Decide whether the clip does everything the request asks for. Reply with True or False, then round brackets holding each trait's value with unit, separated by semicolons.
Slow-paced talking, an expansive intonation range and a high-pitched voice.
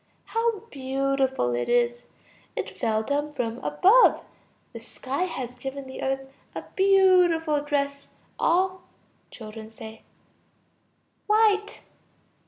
True (100 wpm; 6.9 semitones; 280 Hz)